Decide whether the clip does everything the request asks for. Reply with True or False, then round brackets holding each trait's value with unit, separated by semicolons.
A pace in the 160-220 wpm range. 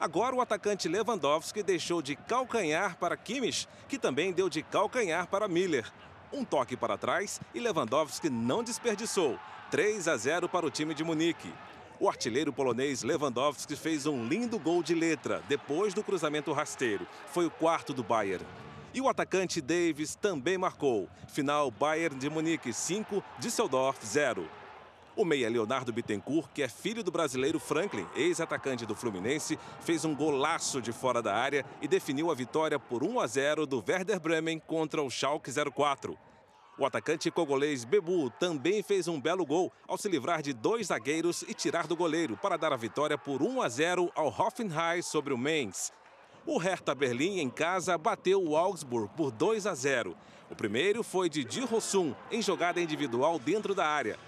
True (170 wpm)